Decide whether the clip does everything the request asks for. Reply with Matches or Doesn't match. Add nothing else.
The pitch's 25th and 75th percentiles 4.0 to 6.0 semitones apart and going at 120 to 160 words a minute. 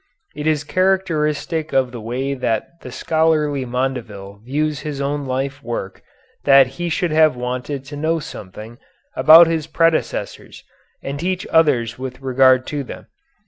Doesn't match